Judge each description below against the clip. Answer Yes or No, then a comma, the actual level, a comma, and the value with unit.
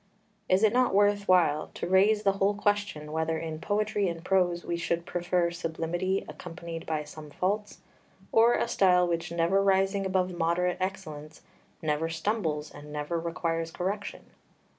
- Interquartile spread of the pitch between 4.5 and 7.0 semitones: No, average, 3.1 semitones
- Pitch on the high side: No, medium, 175 Hz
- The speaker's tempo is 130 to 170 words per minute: Yes, average, 155 wpm